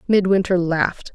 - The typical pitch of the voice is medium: Yes, medium, 180 Hz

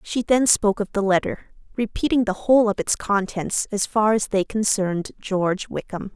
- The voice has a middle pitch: No, high, 210 Hz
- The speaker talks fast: No, average, 185 wpm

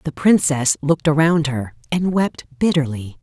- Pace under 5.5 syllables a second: Yes, 4.7 syllables/s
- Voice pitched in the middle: Yes, medium, 150 Hz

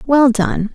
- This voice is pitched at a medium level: No, very high, 255 Hz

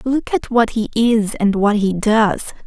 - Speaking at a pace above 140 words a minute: Yes, average, 200 wpm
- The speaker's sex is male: No, female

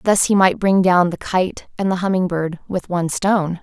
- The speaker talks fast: Yes, fast, 230 wpm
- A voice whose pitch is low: No, medium, 185 Hz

